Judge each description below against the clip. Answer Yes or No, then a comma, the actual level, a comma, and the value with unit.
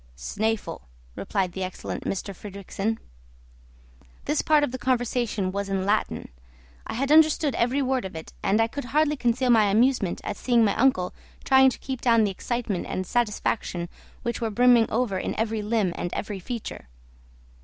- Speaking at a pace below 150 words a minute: No, average, 170 wpm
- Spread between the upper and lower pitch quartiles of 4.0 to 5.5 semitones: Yes, average, 4.3 semitones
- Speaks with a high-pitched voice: Yes, high, 225 Hz